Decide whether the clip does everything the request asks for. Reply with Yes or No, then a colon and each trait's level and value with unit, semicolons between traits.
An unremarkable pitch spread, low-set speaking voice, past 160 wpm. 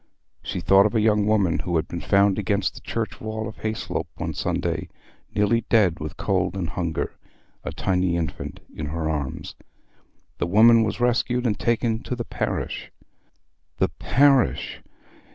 No: average, 4.6 semitones; low, 105 Hz; average, 155 wpm